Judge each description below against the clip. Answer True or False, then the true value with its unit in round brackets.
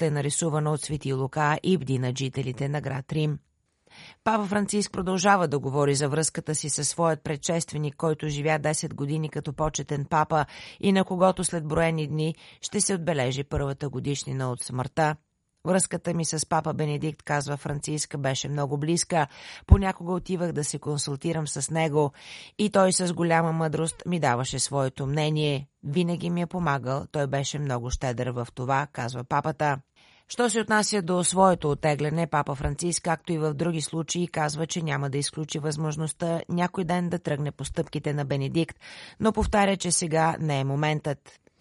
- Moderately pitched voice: True (155 Hz)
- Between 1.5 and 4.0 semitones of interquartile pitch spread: True (3.1 semitones)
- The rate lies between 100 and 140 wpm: False (165 wpm)